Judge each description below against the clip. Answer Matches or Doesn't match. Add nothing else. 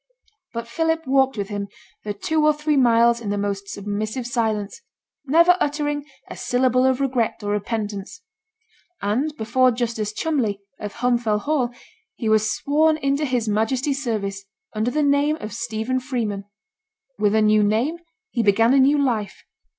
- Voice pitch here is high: Matches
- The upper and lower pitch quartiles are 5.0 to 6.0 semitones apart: Doesn't match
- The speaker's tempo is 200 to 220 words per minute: Doesn't match